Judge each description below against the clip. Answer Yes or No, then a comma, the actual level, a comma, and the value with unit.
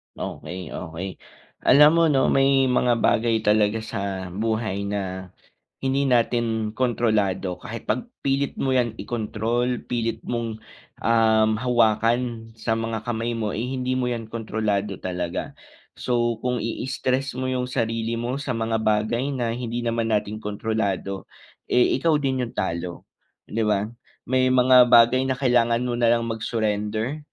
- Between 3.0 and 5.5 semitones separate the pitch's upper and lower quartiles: No, narrow, 2.5 semitones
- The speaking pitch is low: Yes, low, 115 Hz